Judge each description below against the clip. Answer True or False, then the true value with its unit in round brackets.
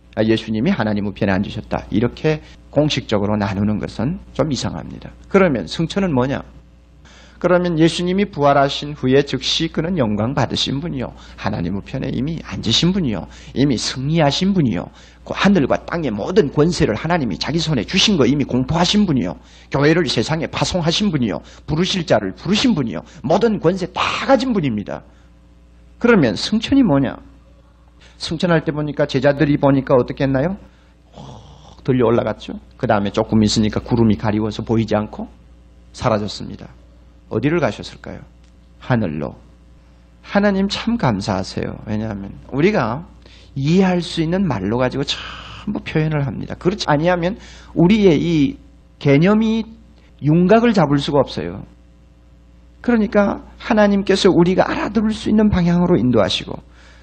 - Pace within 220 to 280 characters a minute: False (330 characters per minute)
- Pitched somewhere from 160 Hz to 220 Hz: False (135 Hz)